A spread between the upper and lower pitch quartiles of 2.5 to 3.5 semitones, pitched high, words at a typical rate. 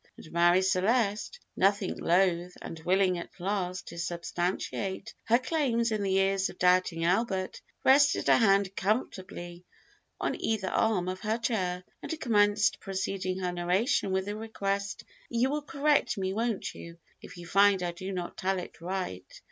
Yes: average, 3.1 semitones; high, 195 Hz; average, 160 wpm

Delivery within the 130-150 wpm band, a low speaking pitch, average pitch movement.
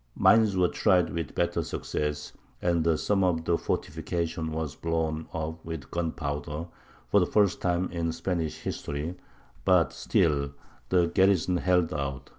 No: average, 140 wpm; very low, 85 Hz; narrow, 2.3 semitones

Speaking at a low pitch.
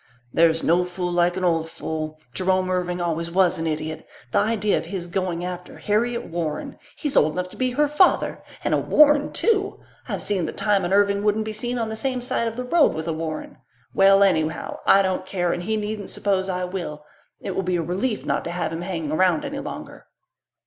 No: medium, 185 Hz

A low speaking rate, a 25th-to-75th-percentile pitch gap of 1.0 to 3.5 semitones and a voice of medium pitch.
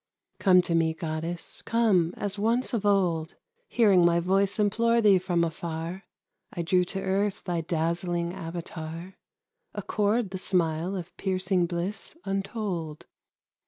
Yes: slow, 130 wpm; average, 2.9 semitones; medium, 180 Hz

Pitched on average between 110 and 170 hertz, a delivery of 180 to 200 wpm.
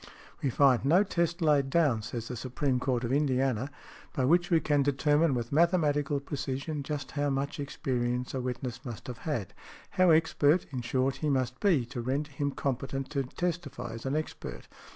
Yes: medium, 140 Hz; average, 185 wpm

